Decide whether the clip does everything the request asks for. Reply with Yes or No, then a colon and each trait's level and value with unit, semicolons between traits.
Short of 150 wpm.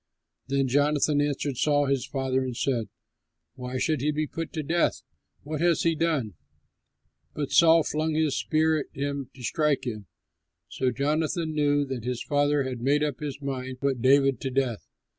No: average, 180 wpm